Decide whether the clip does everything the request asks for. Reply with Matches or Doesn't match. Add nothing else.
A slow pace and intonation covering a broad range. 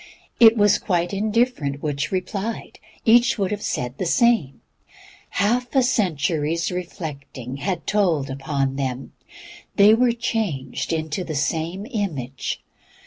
Matches